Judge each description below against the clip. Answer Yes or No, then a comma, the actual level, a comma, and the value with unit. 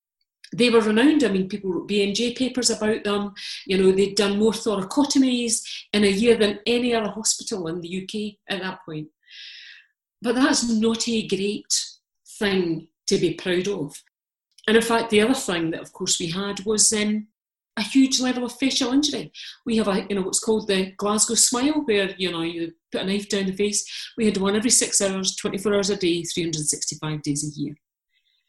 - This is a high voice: Yes, high, 210 Hz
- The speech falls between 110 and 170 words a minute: No, average, 195 wpm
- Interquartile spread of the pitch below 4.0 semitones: Yes, average, 3.6 semitones